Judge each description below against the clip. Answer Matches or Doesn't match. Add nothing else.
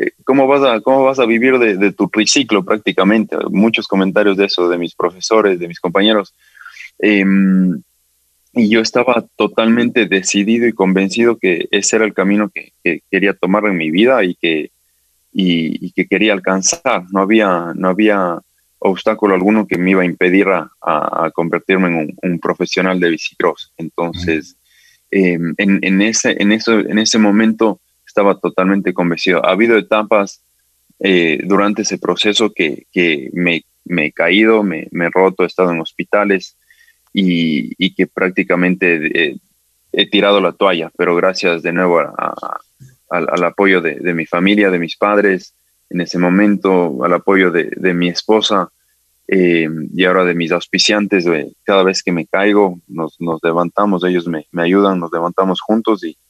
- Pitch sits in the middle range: Doesn't match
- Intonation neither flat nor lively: Matches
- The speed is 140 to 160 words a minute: Doesn't match